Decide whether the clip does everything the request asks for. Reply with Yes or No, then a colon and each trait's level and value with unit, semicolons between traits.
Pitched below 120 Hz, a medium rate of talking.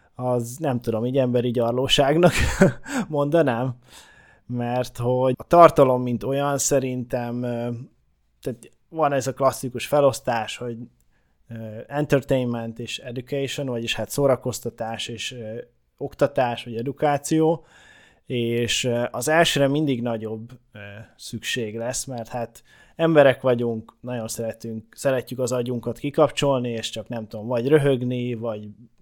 No: low, 125 Hz; average, 115 wpm